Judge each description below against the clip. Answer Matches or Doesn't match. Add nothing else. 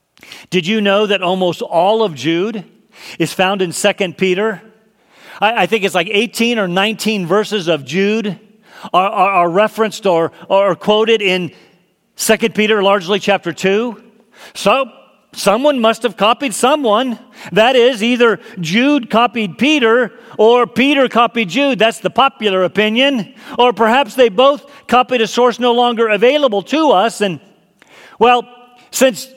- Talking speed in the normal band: Matches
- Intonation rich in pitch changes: Doesn't match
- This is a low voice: Doesn't match